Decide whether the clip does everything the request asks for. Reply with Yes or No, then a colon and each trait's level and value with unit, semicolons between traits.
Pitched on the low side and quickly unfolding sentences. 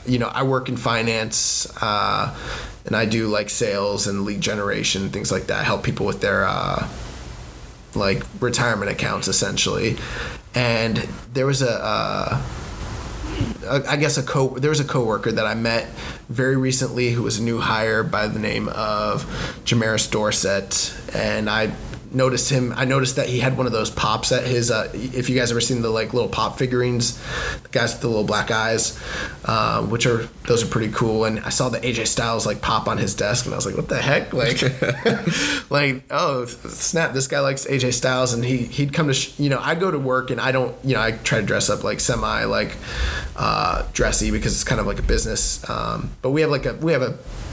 Yes: low, 120 Hz; fast, 210 wpm